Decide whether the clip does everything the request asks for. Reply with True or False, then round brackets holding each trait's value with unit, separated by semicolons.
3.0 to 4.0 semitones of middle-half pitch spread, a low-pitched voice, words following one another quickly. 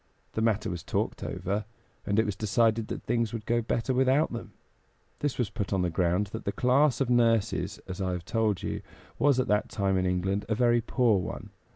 True (3.5 semitones; 110 Hz; 215 wpm)